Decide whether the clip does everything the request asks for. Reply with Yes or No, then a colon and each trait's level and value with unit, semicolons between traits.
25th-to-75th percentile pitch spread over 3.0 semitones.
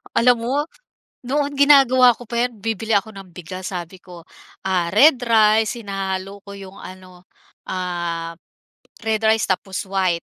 Yes: average, 3.9 semitones